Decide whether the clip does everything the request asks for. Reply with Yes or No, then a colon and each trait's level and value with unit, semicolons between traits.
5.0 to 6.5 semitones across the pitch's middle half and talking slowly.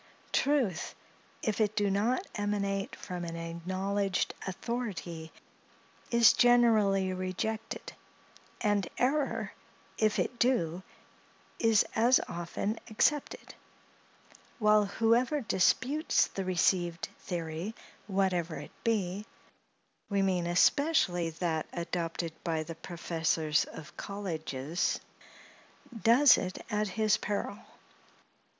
No: average, 4.5 semitones; slow, 90 wpm